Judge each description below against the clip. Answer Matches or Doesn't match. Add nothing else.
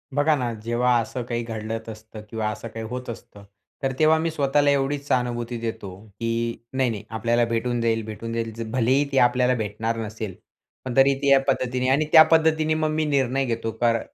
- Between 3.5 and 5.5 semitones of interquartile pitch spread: Doesn't match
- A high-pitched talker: Doesn't match